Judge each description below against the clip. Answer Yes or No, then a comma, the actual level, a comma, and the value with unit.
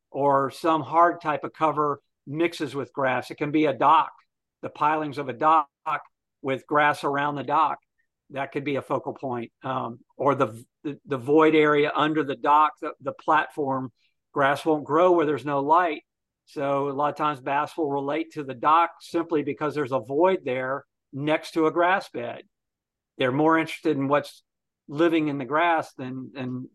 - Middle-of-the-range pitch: Yes, medium, 150 Hz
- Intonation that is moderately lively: No, narrow, 2.2 semitones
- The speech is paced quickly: No, average, 185 wpm